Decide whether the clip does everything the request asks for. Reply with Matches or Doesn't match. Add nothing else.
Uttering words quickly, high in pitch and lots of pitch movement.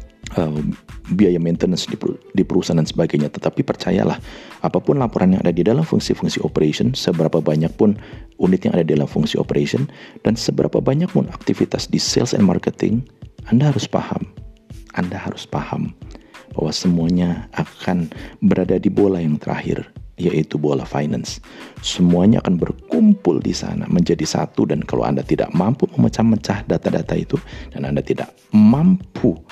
Doesn't match